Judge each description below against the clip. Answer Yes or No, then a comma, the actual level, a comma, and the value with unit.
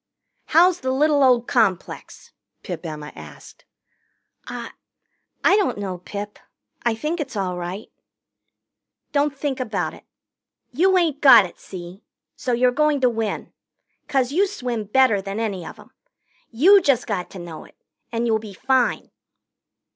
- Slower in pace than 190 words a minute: Yes, average, 150 wpm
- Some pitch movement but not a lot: No, wide, 6.3 semitones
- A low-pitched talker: No, high, 240 Hz